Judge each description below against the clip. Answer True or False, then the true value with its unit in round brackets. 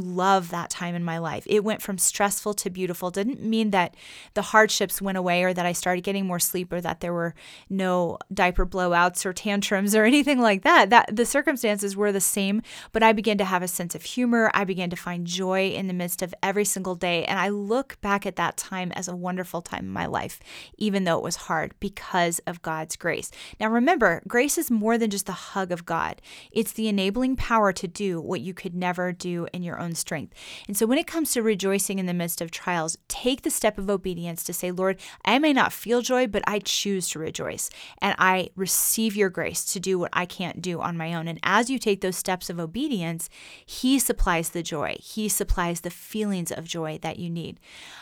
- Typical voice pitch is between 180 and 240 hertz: True (190 Hz)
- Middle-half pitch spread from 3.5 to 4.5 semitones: False (3.1 semitones)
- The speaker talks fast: True (225 wpm)